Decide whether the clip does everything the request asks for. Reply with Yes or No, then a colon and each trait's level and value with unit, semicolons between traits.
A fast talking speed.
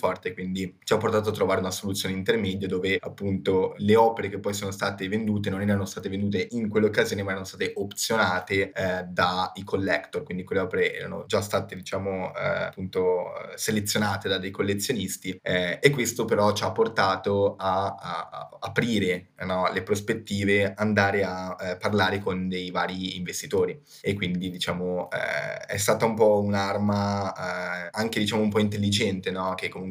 Yes: fast, 175 wpm